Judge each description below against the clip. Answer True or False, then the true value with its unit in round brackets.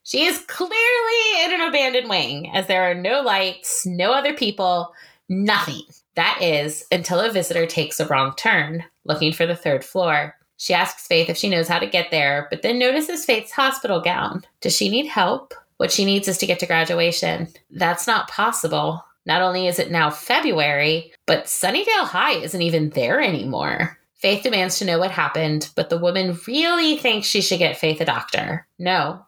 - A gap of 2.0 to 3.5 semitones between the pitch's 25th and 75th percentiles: False (5.5 semitones)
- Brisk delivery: False (190 wpm)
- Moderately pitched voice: True (180 Hz)